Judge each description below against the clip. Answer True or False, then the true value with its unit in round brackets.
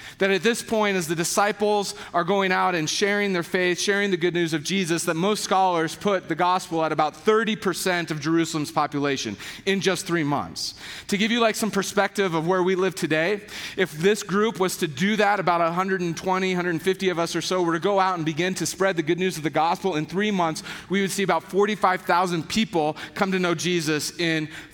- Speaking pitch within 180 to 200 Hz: True (185 Hz)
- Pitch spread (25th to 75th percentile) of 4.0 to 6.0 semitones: False (2.9 semitones)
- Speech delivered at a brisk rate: True (215 wpm)